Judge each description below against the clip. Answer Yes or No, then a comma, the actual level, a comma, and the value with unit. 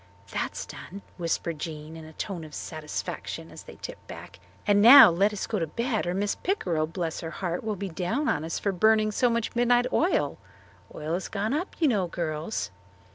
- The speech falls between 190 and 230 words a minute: Yes, average, 200 wpm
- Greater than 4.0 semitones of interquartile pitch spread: Yes, average, 5.3 semitones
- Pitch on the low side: No, high, 190 Hz